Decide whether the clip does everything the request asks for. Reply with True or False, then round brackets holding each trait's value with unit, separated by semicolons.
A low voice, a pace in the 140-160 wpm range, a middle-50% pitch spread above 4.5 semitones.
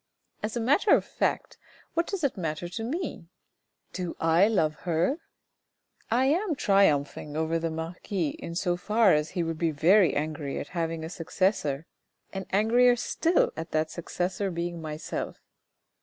False (175 Hz; 155 wpm; 5.4 semitones)